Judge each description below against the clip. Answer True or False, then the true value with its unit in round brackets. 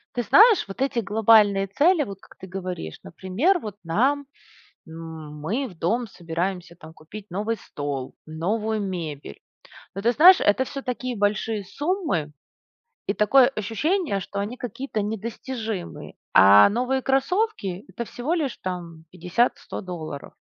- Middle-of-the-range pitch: False (205 Hz)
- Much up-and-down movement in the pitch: True (6.3 semitones)